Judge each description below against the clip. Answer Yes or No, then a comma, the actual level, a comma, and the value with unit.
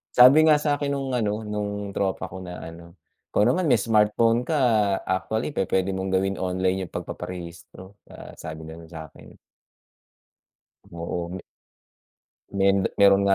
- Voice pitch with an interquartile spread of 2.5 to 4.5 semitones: Yes, average, 3.8 semitones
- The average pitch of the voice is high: No, very low, 95 Hz